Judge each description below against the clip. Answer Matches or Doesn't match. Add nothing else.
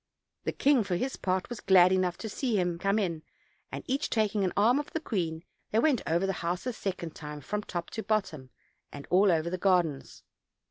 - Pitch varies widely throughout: Doesn't match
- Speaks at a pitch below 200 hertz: Matches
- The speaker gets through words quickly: Matches